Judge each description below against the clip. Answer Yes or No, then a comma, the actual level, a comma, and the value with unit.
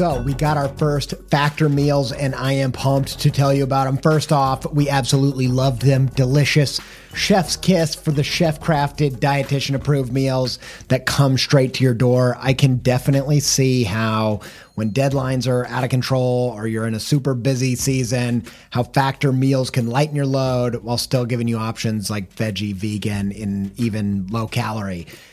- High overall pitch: No, low, 135 Hz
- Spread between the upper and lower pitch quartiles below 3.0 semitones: Yes, narrow, 2.5 semitones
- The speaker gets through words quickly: No, average, 175 wpm